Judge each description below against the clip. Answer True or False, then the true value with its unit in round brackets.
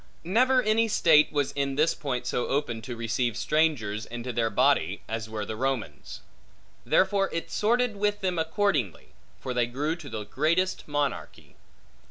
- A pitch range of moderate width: False (7.6 semitones)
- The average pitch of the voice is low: False (145 Hz)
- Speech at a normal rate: True (160 wpm)